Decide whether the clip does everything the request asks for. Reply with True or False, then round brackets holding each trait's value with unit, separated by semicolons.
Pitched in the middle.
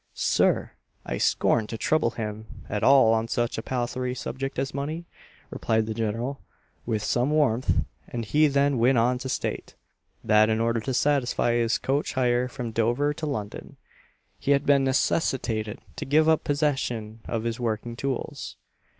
False (120 Hz)